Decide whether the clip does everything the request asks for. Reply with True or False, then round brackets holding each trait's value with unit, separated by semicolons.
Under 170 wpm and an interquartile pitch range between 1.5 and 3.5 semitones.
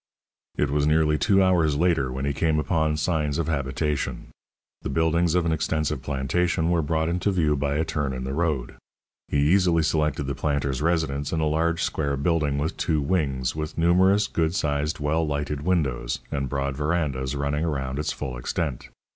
False (180 wpm; 2.8 semitones)